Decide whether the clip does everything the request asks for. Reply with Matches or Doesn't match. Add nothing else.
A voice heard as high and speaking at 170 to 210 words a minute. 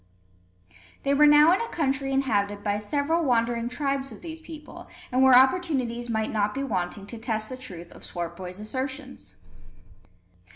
Doesn't match